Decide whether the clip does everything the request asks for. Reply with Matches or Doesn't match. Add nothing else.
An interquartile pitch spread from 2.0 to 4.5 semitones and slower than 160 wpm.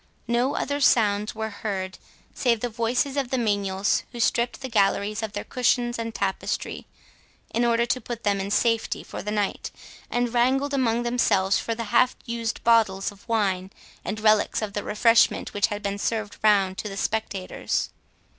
Doesn't match